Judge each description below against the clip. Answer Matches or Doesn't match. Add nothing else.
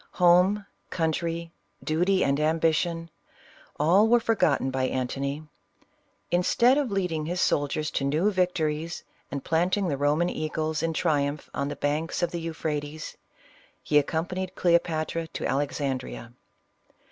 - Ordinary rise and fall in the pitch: Matches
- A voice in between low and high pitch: Matches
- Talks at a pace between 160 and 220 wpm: Doesn't match